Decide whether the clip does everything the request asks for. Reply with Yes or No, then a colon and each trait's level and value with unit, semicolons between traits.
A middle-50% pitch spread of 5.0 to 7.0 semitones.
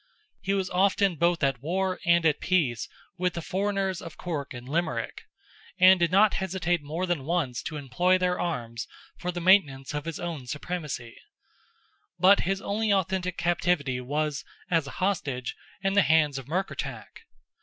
No: average, 4.3 semitones